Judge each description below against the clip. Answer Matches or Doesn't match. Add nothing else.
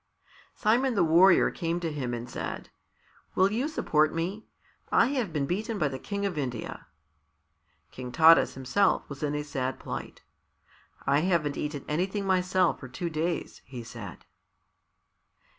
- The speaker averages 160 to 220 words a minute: Doesn't match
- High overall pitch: Doesn't match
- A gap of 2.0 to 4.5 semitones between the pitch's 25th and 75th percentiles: Doesn't match